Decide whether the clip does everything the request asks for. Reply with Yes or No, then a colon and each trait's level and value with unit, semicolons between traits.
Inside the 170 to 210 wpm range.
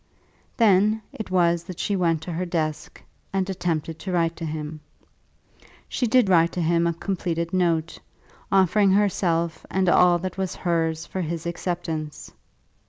No: average, 155 wpm